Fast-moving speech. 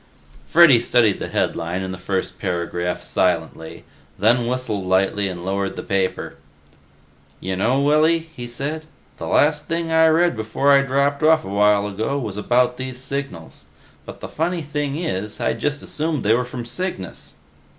No: average, 160 wpm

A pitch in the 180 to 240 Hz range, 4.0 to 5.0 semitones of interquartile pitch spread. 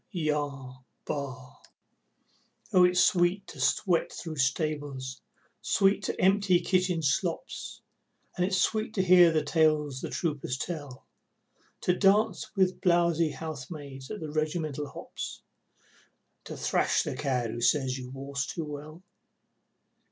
No: medium, 155 Hz; average, 4.6 semitones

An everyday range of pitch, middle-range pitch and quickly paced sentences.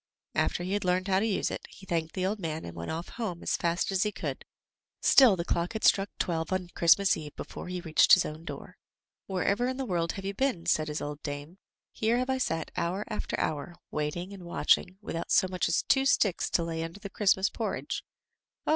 Yes: average, 3.2 semitones; medium, 180 Hz; fast, 230 wpm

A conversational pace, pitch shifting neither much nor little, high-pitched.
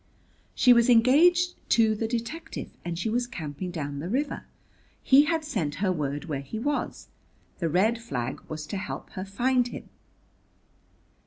No: average, 160 wpm; wide, 7.2 semitones; high, 220 Hz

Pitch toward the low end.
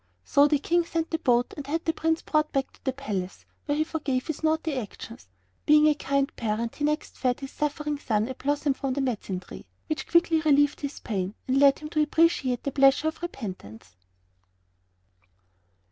No: very high, 280 Hz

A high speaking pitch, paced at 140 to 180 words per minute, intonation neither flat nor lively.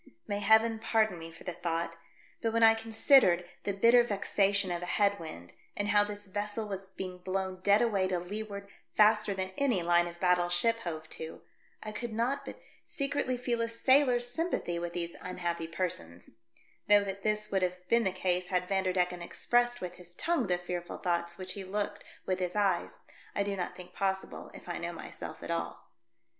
No: high, 195 Hz; average, 195 wpm; average, 3.6 semitones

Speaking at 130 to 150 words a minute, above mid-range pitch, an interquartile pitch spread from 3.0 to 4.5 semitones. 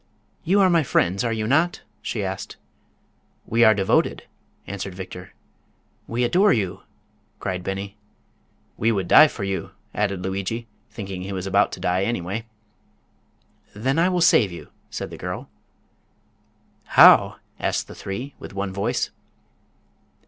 No: average, 140 wpm; low, 100 Hz; average, 3.8 semitones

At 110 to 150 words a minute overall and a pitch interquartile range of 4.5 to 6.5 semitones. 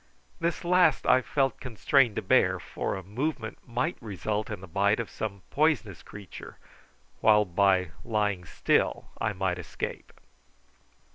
Yes: average, 140 wpm; average, 4.8 semitones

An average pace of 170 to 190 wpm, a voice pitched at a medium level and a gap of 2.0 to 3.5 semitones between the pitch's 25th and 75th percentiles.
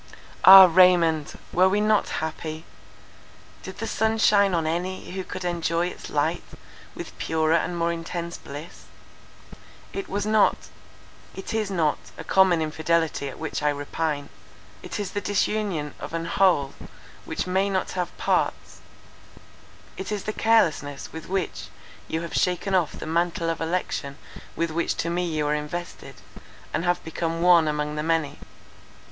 No: average, 155 wpm; medium, 170 Hz; average, 2.9 semitones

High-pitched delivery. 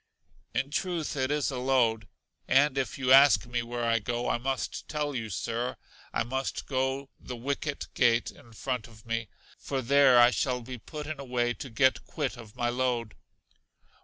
No: low, 125 Hz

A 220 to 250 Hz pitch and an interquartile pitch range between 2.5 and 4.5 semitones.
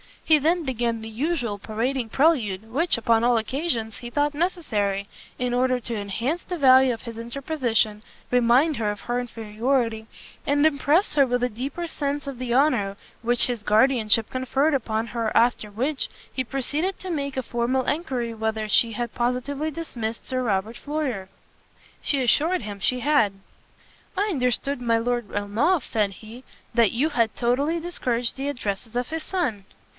Yes: high, 245 Hz; average, 4.1 semitones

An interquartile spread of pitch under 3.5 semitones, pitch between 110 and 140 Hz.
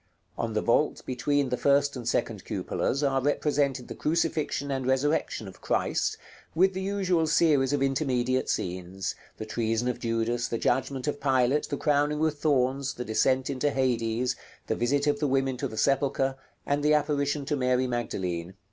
Yes: average, 3.0 semitones; low, 135 Hz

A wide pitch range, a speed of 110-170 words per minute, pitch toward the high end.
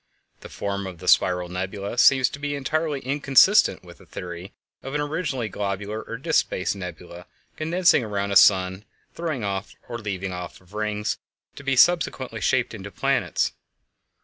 No: wide, 7.0 semitones; average, 160 wpm; low, 105 Hz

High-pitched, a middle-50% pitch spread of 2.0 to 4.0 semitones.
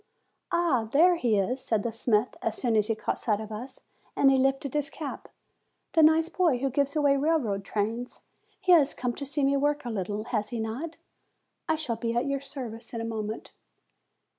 No: very high, 255 Hz; average, 4.5 semitones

